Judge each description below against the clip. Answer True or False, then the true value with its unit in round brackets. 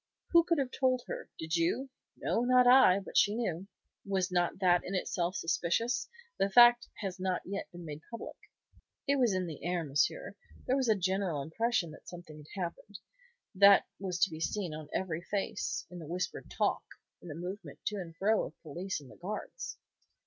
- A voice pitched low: False (190 Hz)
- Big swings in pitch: False (4.6 semitones)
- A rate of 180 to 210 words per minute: True (190 wpm)